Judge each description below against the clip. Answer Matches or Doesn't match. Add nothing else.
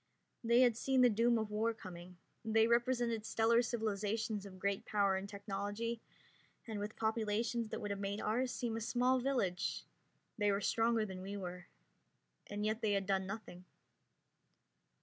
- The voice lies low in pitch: Doesn't match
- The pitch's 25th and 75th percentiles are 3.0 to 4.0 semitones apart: Doesn't match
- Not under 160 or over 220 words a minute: Matches